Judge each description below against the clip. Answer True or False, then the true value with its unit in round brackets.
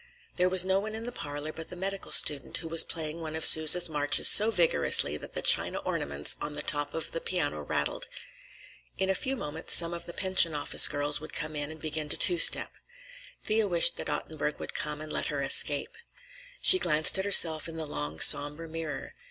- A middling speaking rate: False (210 wpm)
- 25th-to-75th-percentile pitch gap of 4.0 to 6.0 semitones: False (3.3 semitones)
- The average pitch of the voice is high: False (160 Hz)